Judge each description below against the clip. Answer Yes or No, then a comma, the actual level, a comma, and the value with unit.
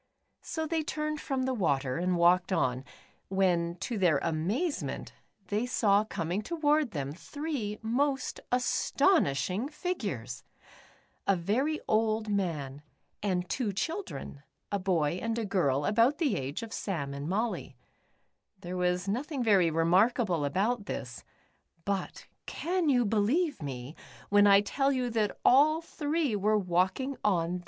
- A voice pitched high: Yes, high, 205 Hz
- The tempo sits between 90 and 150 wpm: Yes, slow, 135 wpm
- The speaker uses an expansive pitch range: Yes, wide, 7.0 semitones